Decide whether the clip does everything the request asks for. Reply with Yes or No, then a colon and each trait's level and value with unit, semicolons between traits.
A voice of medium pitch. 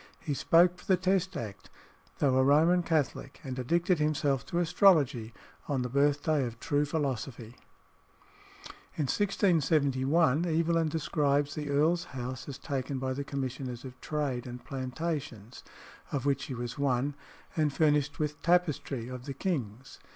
Yes: medium, 145 Hz